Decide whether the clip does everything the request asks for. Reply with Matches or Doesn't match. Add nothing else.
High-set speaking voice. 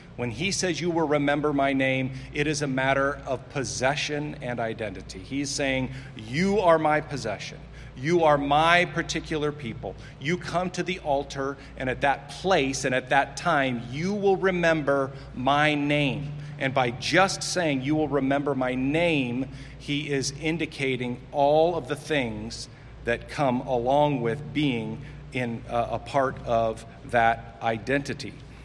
Doesn't match